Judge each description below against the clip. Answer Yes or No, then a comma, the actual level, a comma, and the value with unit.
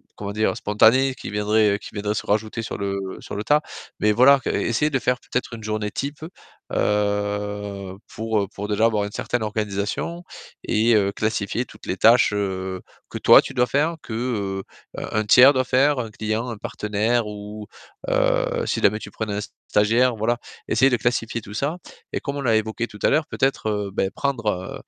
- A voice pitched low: Yes, low, 110 Hz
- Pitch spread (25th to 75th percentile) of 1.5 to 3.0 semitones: No, average, 3.4 semitones